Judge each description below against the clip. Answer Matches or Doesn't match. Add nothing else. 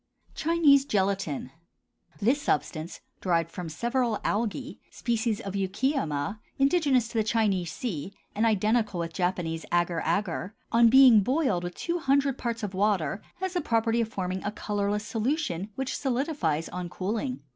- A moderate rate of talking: Matches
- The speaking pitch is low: Doesn't match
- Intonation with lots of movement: Matches